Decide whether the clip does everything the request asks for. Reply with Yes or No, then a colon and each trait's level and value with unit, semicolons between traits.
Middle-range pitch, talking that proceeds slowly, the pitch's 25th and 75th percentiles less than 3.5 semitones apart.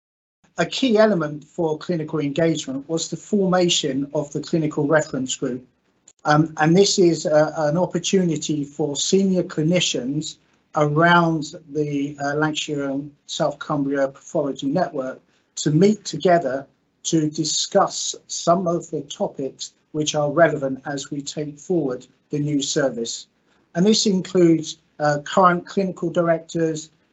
Yes: medium, 155 Hz; slow, 130 wpm; average, 2.9 semitones